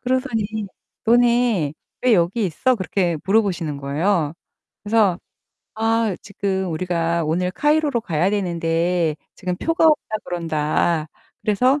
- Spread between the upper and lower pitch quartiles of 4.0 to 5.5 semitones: Yes, average, 5.2 semitones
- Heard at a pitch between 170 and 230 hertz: Yes, high, 190 Hz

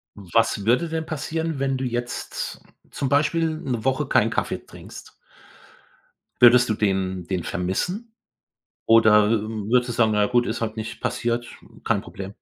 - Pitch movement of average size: Yes, average, 4.0 semitones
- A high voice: No, low, 120 Hz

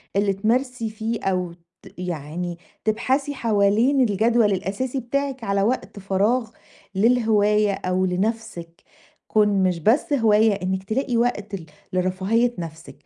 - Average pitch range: Yes, average, 3.9 semitones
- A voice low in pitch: No, high, 210 Hz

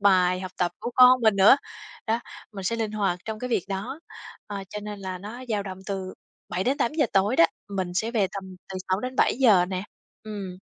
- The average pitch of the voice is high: Yes, high, 205 Hz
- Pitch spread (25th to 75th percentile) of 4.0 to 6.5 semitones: No, average, 3.3 semitones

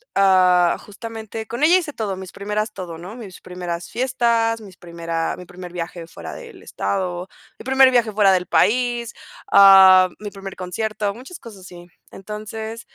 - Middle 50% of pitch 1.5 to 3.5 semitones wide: No, average, 3.9 semitones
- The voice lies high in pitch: Yes, high, 200 Hz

